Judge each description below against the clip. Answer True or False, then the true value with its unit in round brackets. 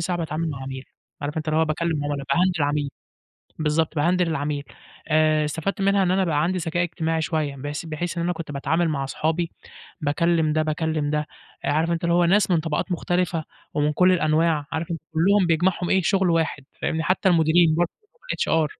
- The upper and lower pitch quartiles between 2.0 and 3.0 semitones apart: True (2.4 semitones)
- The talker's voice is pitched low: False (160 Hz)